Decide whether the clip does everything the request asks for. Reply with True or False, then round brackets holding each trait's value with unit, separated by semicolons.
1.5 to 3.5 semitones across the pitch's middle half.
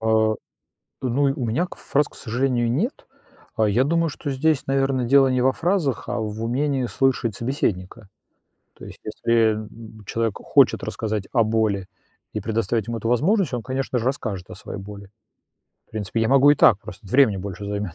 False (4.1 semitones)